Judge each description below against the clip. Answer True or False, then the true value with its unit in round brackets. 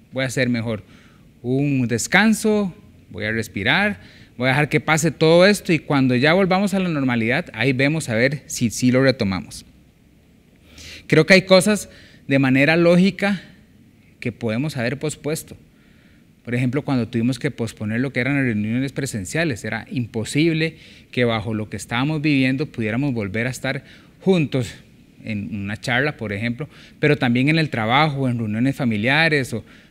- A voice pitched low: True (130 Hz)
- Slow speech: False (165 wpm)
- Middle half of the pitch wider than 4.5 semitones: True (5.1 semitones)